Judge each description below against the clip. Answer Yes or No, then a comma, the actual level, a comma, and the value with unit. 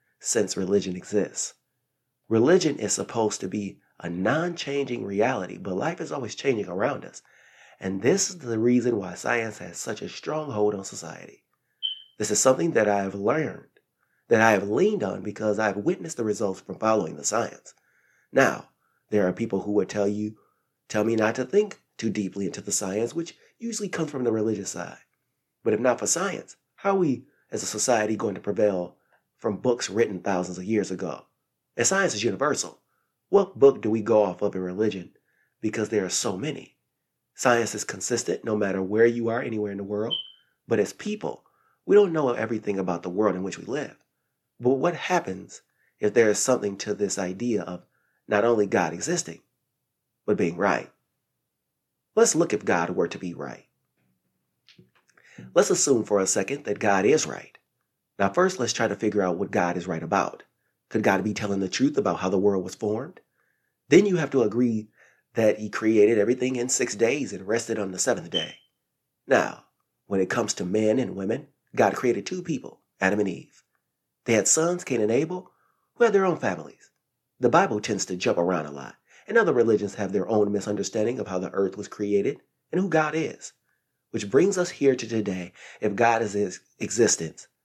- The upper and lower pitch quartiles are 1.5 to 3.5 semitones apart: No, average, 4.0 semitones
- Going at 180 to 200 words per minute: Yes, average, 195 wpm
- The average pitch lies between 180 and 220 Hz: No, low, 105 Hz